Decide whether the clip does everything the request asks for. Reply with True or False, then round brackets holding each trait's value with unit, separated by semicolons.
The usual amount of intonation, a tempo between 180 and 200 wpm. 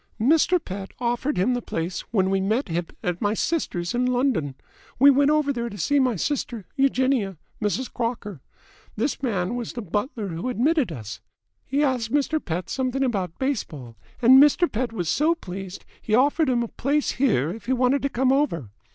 False (6.0 semitones; 190 wpm)